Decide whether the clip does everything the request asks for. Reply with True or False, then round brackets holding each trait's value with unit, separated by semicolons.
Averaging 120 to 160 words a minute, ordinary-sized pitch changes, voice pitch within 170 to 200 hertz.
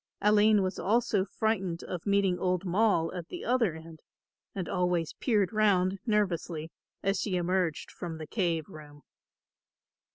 True (140 wpm; 3.6 semitones; 185 Hz)